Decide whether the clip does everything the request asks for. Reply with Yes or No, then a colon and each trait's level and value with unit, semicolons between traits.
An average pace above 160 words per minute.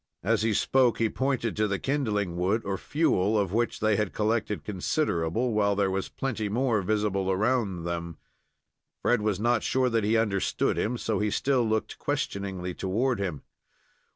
Yes: average, 170 wpm